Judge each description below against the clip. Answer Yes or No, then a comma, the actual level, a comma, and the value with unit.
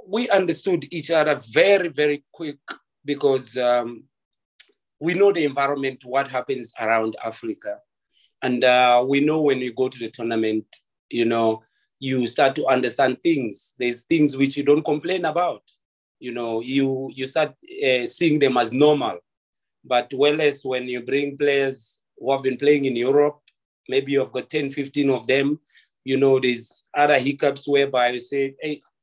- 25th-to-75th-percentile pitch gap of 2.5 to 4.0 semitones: Yes, average, 3.0 semitones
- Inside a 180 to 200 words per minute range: No, average, 165 wpm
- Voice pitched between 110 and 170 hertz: Yes, medium, 140 Hz